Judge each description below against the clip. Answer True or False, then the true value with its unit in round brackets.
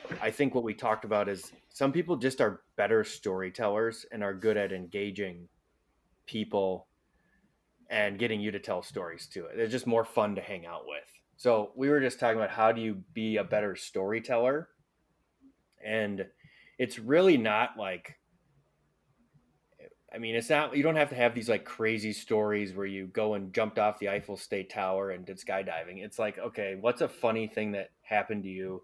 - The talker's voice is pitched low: True (110 Hz)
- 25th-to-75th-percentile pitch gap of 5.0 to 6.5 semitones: False (3.2 semitones)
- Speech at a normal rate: True (185 wpm)